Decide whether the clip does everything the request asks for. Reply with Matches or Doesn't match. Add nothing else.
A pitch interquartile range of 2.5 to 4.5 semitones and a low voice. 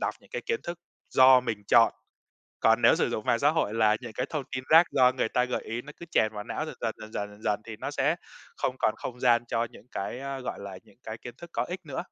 Matches